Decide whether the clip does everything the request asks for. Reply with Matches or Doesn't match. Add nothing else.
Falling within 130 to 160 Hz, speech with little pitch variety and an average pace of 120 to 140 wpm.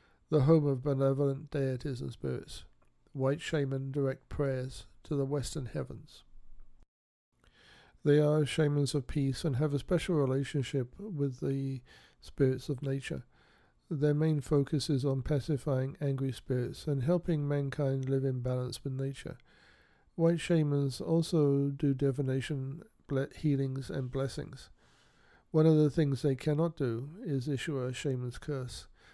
Matches